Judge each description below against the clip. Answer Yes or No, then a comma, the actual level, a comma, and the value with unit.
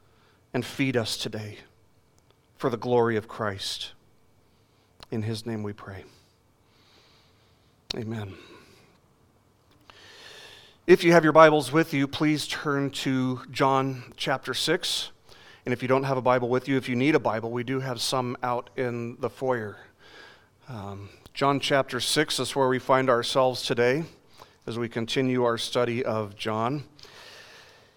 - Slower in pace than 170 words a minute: Yes, average, 145 wpm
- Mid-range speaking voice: No, low, 125 Hz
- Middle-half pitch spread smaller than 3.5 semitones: Yes, average, 3.0 semitones